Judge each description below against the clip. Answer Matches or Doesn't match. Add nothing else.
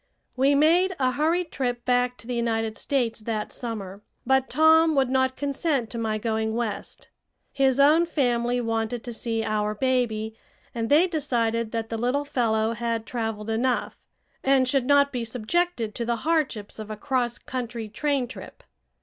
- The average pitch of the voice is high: Matches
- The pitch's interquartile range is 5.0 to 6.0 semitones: Doesn't match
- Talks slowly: Doesn't match